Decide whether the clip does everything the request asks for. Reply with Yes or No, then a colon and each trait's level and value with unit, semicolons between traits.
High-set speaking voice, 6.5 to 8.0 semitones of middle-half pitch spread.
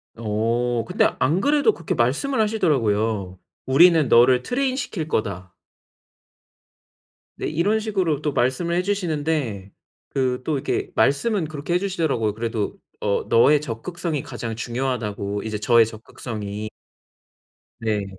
No: low, 130 Hz; wide, 7.4 semitones